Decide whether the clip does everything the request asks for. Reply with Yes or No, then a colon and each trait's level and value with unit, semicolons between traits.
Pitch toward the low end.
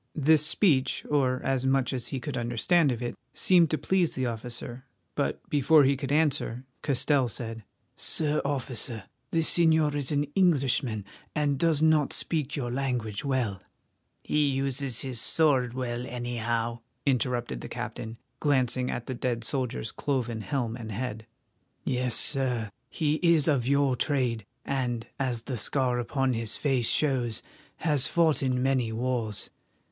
Yes: low, 130 Hz